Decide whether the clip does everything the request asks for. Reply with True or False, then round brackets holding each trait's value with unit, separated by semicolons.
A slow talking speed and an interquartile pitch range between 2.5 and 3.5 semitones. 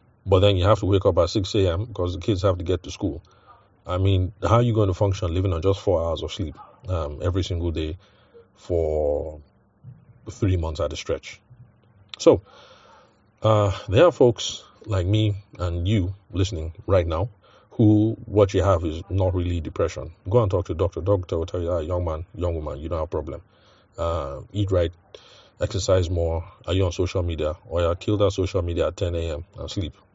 False (205 wpm; 2.8 semitones)